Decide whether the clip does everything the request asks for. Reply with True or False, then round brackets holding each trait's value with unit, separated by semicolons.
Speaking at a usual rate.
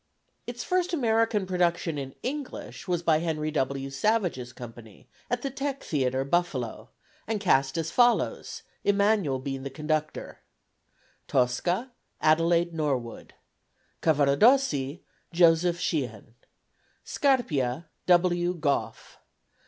False (105 wpm)